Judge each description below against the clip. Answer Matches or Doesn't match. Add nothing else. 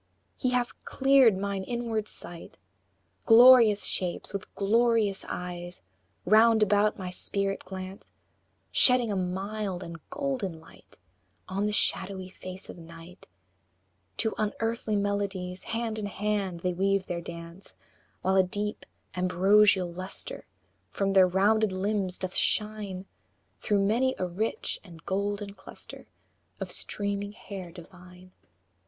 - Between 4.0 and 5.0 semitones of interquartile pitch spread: Doesn't match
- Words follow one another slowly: Matches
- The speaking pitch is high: Matches